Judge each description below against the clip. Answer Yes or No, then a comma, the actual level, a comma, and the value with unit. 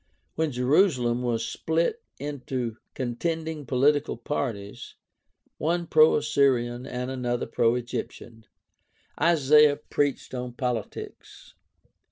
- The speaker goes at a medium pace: No, slow, 95 wpm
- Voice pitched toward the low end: Yes, low, 130 Hz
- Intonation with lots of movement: No, average, 3.8 semitones